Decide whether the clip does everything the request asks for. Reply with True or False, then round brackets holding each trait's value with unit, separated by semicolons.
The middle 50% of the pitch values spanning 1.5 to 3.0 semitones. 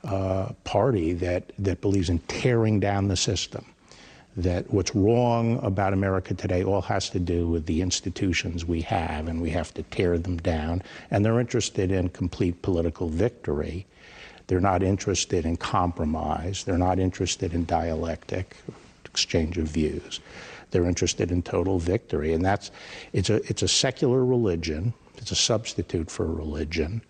True (2.6 semitones)